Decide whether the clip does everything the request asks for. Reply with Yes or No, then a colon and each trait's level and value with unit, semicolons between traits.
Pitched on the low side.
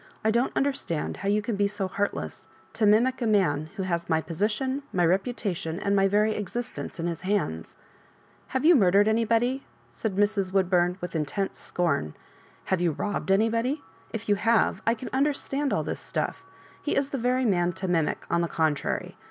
No: high, 205 Hz